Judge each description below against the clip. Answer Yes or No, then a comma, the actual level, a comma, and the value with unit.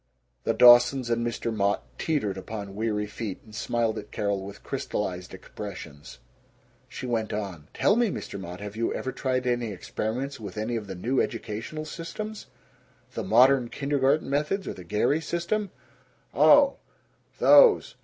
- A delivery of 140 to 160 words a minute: Yes, average, 155 wpm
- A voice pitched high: No, low, 115 Hz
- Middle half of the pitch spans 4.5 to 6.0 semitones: Yes, average, 5.1 semitones